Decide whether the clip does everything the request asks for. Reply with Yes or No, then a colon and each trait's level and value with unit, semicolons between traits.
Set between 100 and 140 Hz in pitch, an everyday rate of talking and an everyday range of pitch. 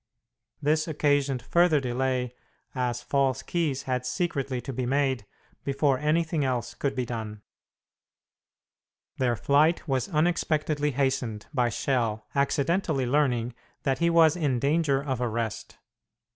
No: low, 135 Hz; slow, 125 wpm; average, 3.3 semitones